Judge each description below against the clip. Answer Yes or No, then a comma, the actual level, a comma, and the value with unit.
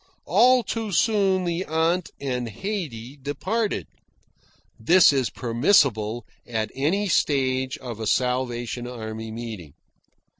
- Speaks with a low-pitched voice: Yes, low, 130 Hz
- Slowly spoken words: Yes, slow, 110 wpm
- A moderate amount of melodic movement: No, wide, 7.7 semitones